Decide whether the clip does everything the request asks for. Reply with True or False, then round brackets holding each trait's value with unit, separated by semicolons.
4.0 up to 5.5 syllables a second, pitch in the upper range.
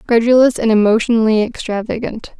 False (6.0 syllables/s; 225 Hz)